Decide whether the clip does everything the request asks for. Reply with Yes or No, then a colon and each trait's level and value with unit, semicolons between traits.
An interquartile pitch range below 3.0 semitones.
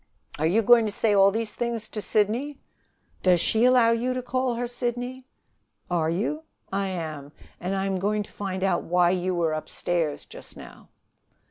No: average, 5.0 semitones